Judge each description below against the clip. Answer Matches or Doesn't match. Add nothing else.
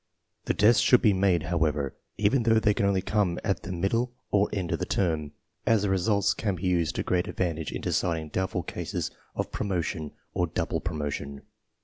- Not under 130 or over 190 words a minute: Doesn't match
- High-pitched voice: Doesn't match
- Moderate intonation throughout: Matches